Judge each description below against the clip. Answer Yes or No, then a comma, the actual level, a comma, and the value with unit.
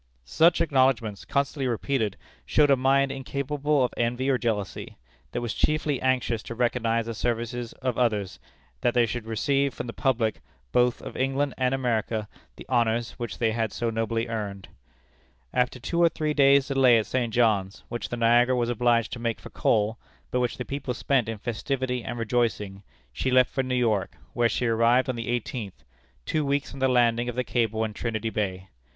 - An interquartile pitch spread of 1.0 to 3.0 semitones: Yes, narrow, 2.5 semitones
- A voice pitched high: No, low, 120 Hz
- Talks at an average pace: Yes, average, 190 wpm